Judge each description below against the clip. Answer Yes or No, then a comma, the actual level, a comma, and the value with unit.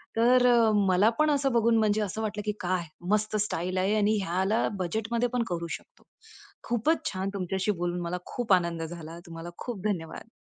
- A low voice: No, high, 205 Hz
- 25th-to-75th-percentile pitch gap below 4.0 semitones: No, average, 4.3 semitones